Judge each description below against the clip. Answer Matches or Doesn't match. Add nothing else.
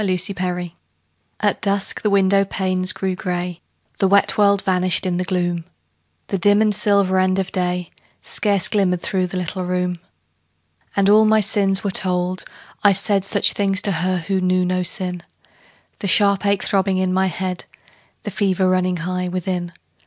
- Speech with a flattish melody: Matches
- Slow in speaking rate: Doesn't match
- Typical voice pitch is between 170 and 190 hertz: Matches